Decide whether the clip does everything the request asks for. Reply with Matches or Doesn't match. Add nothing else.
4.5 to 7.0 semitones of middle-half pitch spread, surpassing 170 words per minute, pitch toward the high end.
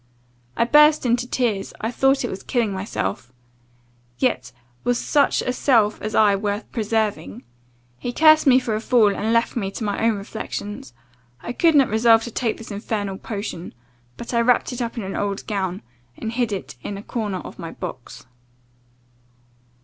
Doesn't match